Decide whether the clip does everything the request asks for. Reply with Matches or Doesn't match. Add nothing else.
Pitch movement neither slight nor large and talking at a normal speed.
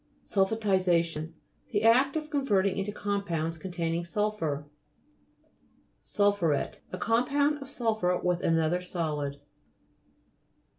Doesn't match